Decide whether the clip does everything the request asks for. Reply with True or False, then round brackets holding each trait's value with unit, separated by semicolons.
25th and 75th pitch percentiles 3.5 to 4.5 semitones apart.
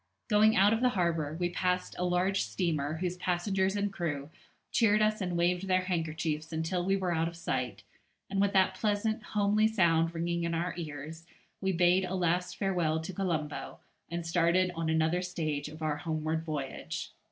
False (2.9 semitones)